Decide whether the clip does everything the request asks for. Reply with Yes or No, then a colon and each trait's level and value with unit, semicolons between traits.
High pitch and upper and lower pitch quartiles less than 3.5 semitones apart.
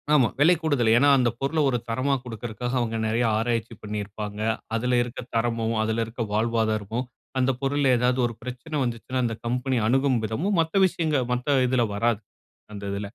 No: low, 120 Hz; average, 2.8 semitones